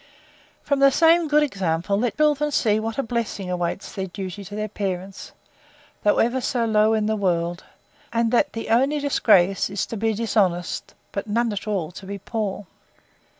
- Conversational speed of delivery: Yes, average, 180 wpm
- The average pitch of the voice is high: Yes, high, 215 Hz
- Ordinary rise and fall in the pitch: Yes, average, 3.6 semitones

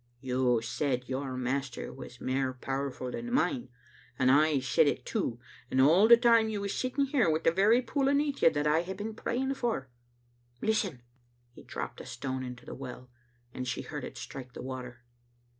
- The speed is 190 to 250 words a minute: Yes, average, 195 wpm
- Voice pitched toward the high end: No, medium, 140 Hz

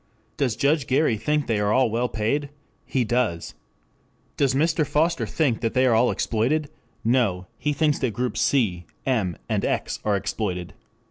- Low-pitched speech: Yes, low, 125 Hz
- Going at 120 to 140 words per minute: No, average, 160 wpm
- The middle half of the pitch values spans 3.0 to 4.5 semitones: No, average, 4.9 semitones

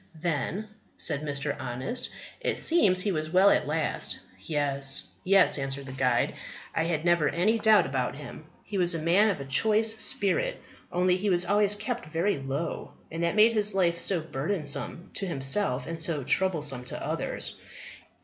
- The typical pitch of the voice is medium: Yes, medium, 170 Hz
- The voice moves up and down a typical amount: No, wide, 5.8 semitones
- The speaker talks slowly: No, average, 170 wpm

